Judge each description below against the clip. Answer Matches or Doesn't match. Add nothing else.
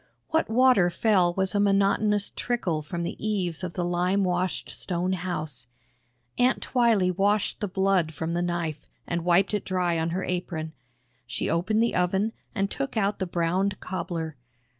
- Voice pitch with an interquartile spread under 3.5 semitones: Matches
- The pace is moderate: Matches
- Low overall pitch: Doesn't match